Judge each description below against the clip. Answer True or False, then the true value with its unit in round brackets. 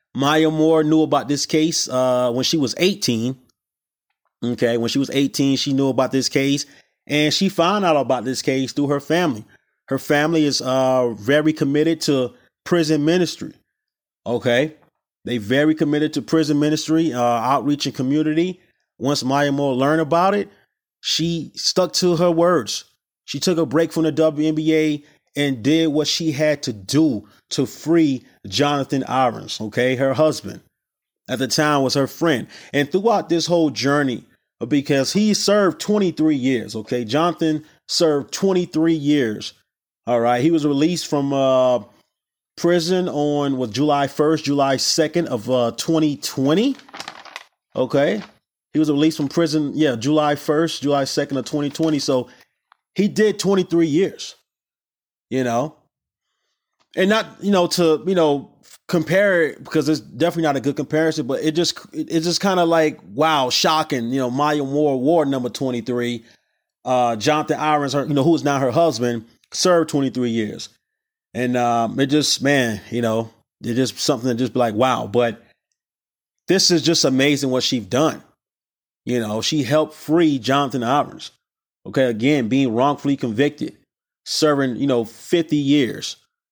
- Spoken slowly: False (160 wpm)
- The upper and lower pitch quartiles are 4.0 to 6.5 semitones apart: False (3.5 semitones)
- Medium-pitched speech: True (145 Hz)